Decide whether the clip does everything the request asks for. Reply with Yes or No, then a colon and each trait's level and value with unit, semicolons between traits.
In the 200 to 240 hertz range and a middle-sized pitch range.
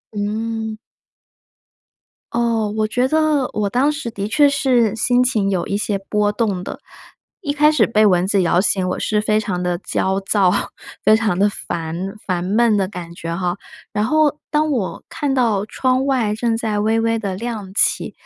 Yes: high, 215 Hz; average, 3.9 semitones